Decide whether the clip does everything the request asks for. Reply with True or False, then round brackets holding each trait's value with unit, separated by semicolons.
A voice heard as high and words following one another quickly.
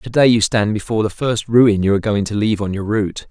False (105 Hz; 290 wpm)